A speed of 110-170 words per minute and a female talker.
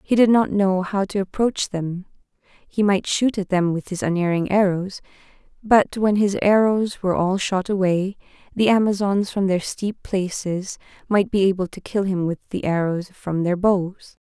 No: average, 180 wpm; female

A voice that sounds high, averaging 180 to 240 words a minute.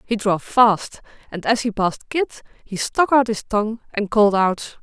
Yes: high, 215 Hz; average, 200 wpm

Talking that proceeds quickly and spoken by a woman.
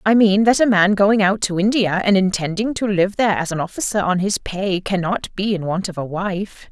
Yes: fast, 240 wpm; female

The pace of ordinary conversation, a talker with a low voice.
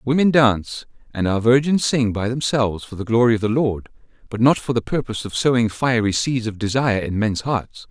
No: fast, 220 wpm; low, 120 Hz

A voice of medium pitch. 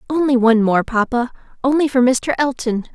No: very high, 250 Hz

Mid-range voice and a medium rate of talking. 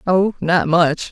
Yes: medium, 175 Hz; average, 160 wpm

